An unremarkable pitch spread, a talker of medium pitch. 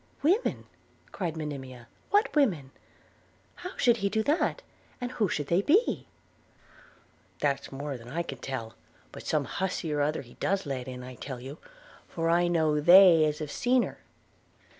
No: wide, 6.4 semitones; medium, 160 Hz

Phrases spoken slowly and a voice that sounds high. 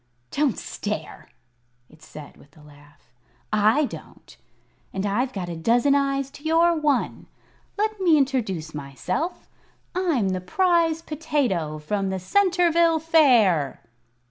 Yes: slow, 125 wpm; very high, 255 Hz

